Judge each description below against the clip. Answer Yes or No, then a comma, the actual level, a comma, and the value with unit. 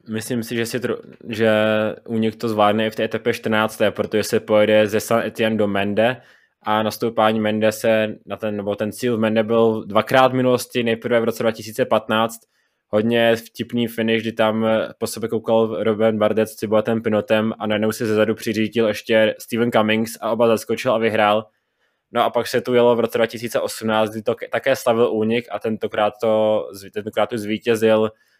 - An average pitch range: No, narrow, 1.1 semitones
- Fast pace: Yes, fast, 180 wpm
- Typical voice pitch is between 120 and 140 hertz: No, low, 110 Hz